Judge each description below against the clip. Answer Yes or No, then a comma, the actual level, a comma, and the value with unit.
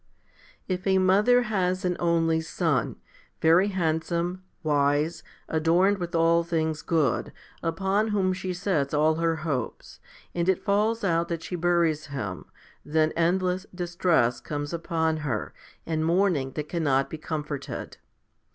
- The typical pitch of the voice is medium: Yes, medium, 165 Hz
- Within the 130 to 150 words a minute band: Yes, average, 140 wpm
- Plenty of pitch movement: No, average, 2.9 semitones